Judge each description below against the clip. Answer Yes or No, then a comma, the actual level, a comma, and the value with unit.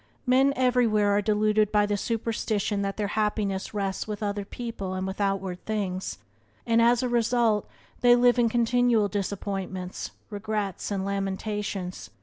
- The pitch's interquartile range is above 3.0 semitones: No, average, 2.7 semitones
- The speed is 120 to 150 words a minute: Yes, average, 145 wpm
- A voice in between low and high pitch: No, high, 210 Hz